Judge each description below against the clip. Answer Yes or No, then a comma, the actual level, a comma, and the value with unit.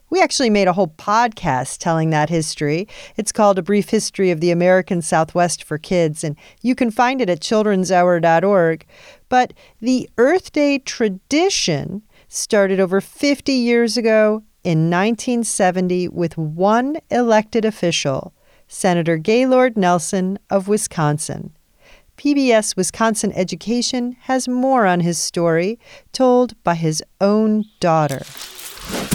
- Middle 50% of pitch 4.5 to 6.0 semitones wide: Yes, wide, 5.4 semitones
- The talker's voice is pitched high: Yes, high, 200 Hz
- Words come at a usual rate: No, slow, 125 wpm